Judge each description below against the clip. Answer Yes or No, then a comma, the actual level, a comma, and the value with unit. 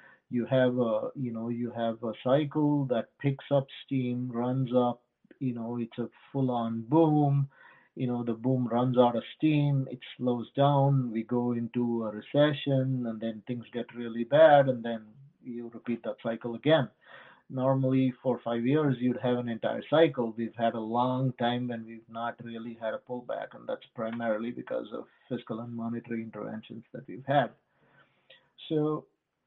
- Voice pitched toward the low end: Yes, low, 120 Hz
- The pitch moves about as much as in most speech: No, narrow, 2.1 semitones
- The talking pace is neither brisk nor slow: Yes, average, 170 wpm